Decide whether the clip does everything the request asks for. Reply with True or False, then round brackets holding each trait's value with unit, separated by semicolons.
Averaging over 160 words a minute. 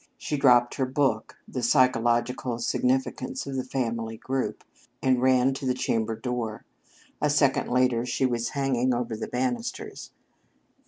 False (145 wpm)